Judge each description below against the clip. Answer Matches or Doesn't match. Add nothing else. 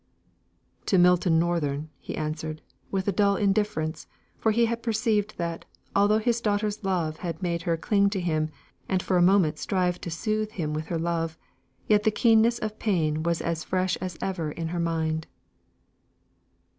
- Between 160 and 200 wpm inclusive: Matches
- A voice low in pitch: Doesn't match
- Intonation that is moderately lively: Matches